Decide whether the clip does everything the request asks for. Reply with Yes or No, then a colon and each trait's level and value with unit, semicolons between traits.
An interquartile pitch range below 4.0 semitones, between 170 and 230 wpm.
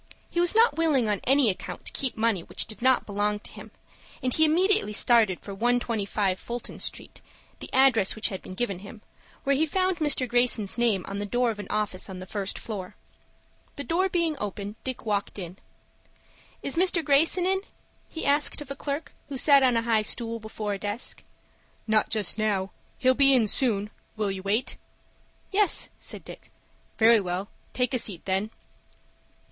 No: average, 5.3 semitones; average, 185 wpm